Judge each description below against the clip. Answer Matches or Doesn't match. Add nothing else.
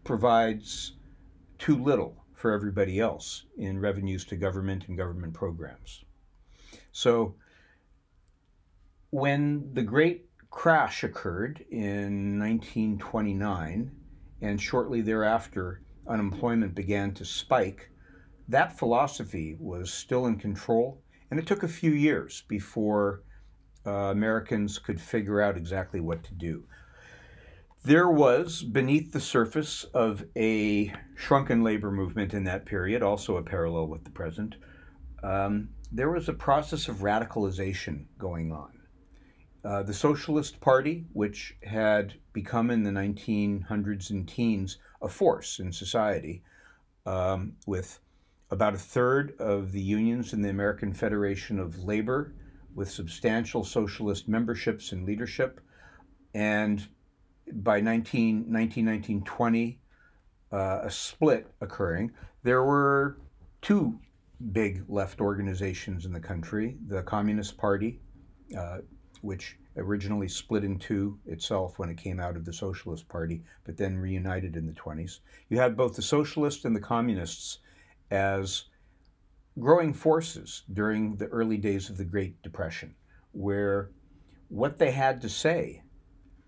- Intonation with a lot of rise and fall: Doesn't match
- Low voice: Matches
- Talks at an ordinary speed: Doesn't match